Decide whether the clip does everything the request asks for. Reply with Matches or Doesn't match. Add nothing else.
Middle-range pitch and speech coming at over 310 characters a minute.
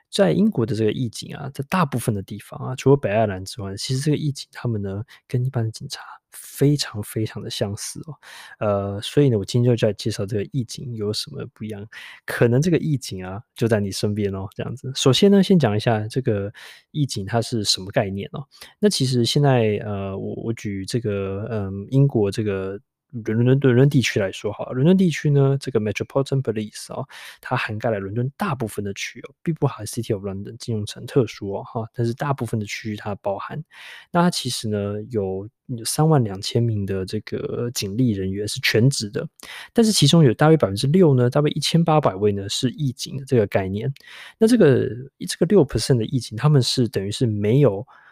Doesn't match